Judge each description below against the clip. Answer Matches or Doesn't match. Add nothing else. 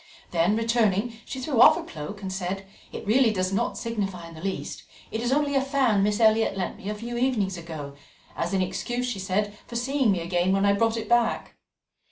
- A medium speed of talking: Doesn't match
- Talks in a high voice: Matches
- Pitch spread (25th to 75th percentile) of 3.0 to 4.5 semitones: Matches